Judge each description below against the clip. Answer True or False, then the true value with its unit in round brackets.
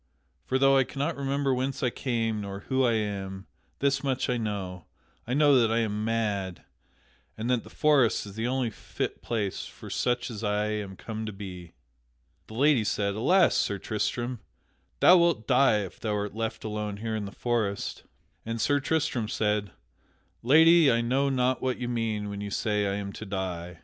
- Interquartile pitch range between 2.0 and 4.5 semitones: True (4.1 semitones)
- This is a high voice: False (115 Hz)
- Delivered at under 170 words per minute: False (190 wpm)